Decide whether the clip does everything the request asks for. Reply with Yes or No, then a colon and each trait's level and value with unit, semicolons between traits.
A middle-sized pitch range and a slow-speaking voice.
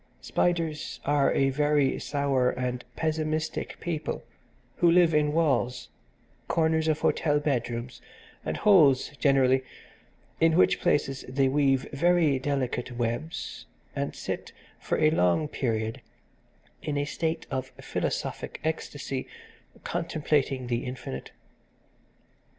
Yes: average, 3.5 semitones; slow, 110 wpm